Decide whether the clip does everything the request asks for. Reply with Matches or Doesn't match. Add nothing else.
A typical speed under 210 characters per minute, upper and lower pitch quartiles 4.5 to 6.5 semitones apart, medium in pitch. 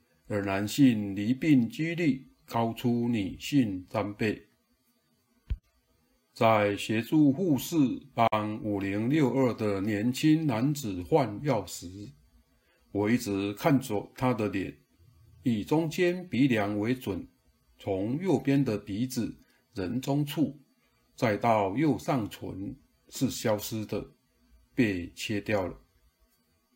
Doesn't match